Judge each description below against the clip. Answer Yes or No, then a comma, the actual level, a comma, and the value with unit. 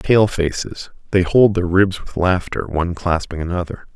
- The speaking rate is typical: Yes, average, 150 wpm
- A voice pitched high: No, very low, 90 Hz